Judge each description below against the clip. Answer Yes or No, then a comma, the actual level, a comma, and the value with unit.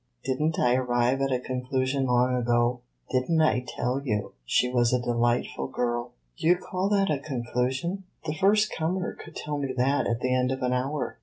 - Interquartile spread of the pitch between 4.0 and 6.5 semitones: No, average, 3.4 semitones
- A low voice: Yes, low, 130 Hz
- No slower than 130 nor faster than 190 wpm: No, fast, 205 wpm